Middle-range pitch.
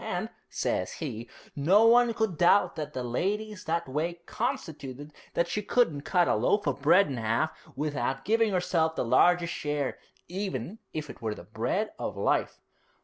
Yes: medium, 160 Hz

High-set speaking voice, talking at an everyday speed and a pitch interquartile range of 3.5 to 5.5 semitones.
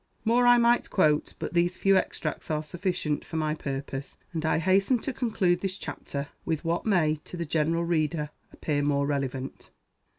No: medium, 165 Hz; average, 175 wpm; average, 3.9 semitones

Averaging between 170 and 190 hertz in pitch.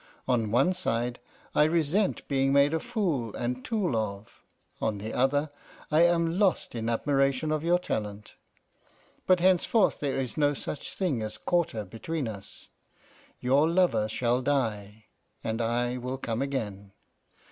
No: low, 135 Hz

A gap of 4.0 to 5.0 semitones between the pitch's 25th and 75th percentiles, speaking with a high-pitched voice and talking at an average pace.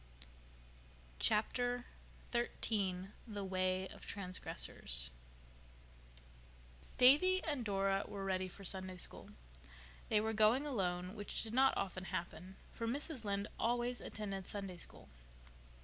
No: average, 4.3 semitones; high, 200 Hz; slow, 115 wpm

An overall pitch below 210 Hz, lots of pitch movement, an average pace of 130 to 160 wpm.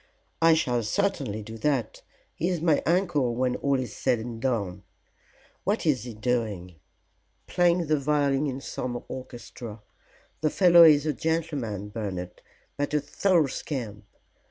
Yes: low, 135 Hz; wide, 5.7 semitones; average, 145 wpm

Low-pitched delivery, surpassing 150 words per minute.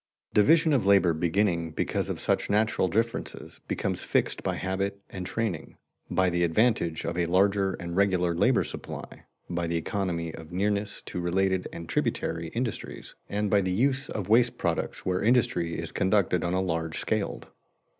Yes: very low, 95 Hz; average, 165 wpm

